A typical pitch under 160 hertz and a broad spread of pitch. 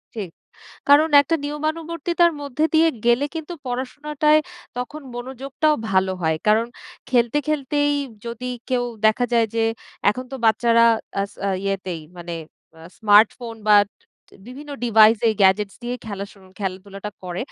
No: high, 240 Hz; wide, 5.8 semitones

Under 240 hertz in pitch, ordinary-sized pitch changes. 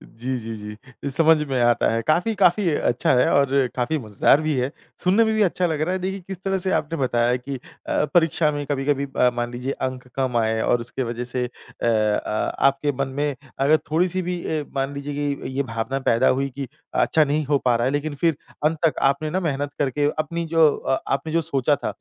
Yes: medium, 140 Hz; average, 3.9 semitones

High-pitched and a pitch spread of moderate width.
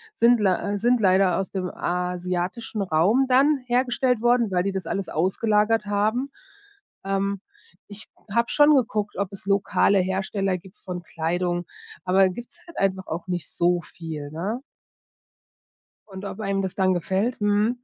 Yes: high, 195 Hz; average, 3.7 semitones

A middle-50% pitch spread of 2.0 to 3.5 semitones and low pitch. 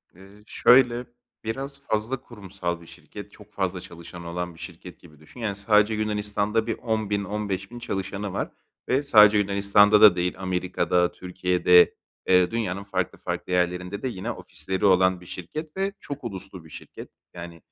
Yes: average, 3.1 semitones; low, 100 Hz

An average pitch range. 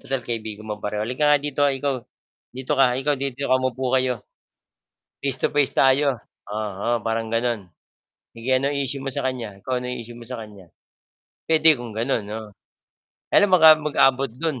Yes: average, 3.3 semitones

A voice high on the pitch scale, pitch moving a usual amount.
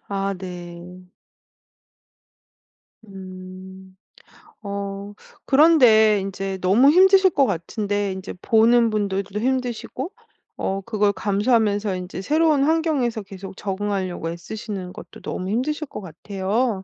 Yes: high, 200 Hz; average, 4.0 semitones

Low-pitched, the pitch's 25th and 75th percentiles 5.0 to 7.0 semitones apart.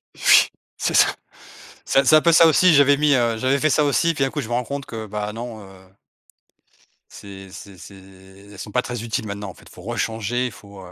Yes: low, 115 Hz; wide, 5.6 semitones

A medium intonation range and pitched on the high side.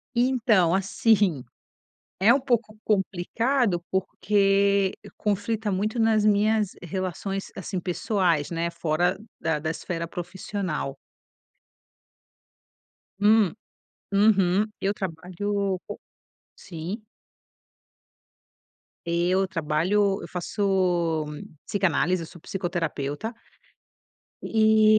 Yes: average, 3.4 semitones; high, 195 Hz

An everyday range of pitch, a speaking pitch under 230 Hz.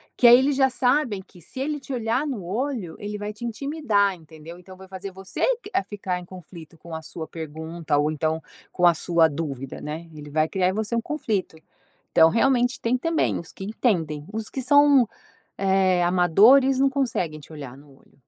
No: wide, 7.3 semitones; high, 190 Hz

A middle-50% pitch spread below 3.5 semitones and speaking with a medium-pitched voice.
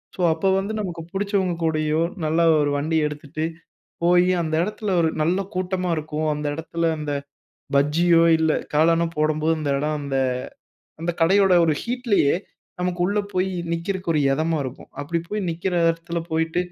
Yes: average, 2.9 semitones; medium, 165 Hz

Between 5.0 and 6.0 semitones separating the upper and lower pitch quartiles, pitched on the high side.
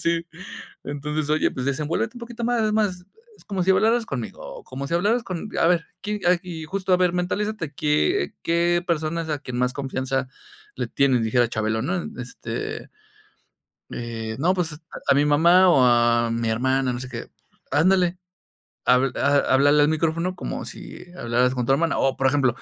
No: wide, 5.6 semitones; medium, 155 Hz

